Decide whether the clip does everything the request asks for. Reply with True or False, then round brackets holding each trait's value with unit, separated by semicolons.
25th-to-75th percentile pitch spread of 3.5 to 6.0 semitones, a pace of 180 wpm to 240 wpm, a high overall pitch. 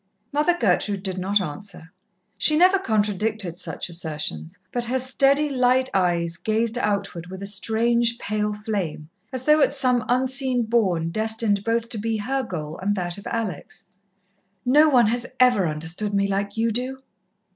False (4.7 semitones; 160 wpm; 215 Hz)